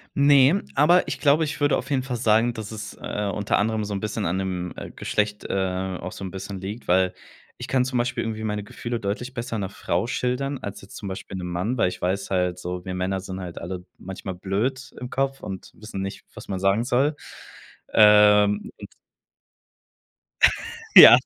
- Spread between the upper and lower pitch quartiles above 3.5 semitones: Yes, average, 4.7 semitones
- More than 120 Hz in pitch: No, low, 105 Hz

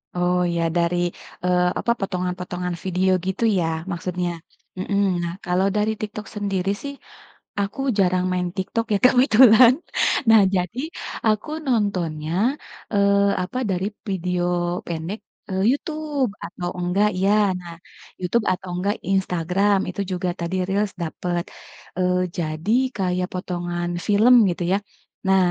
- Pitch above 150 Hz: Yes, medium, 185 Hz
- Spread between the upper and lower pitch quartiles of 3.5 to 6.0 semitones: No, narrow, 2.5 semitones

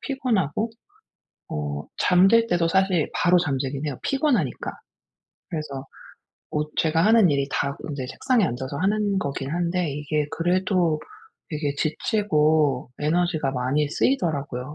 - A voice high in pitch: No, medium, 155 Hz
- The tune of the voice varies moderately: Yes, average, 4.8 semitones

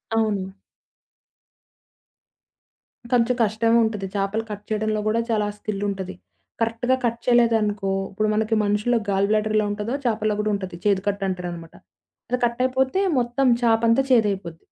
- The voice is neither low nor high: No, high, 215 Hz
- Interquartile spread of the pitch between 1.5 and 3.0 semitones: Yes, narrow, 2.4 semitones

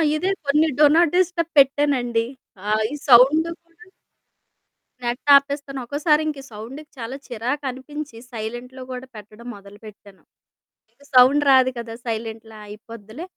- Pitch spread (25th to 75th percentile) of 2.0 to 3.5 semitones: No, average, 4.4 semitones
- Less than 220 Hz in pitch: No, very high, 255 Hz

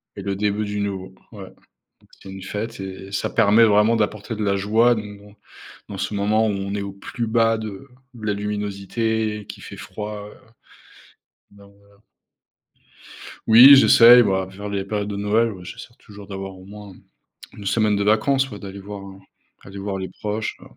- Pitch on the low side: Yes, low, 105 Hz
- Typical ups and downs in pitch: No, narrow, 1.6 semitones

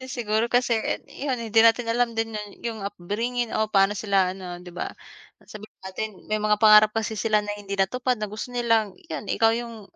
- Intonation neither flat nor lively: No, narrow, 2.2 semitones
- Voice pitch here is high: Yes, high, 215 Hz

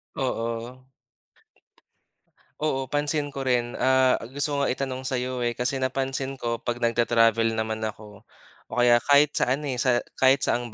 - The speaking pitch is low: Yes, low, 125 Hz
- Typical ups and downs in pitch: No, narrow, 2.3 semitones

